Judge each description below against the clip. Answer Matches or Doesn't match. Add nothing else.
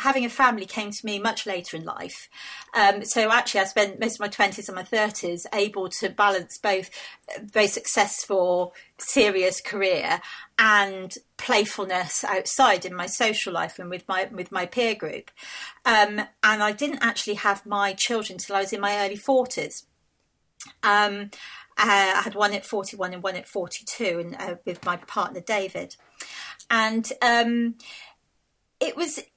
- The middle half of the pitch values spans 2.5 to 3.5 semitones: Matches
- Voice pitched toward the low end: Doesn't match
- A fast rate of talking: Doesn't match